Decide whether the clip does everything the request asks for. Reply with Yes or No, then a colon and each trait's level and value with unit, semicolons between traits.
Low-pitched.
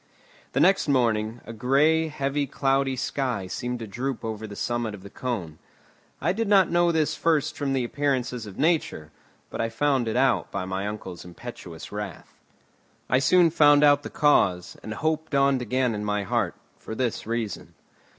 Yes: low, 125 Hz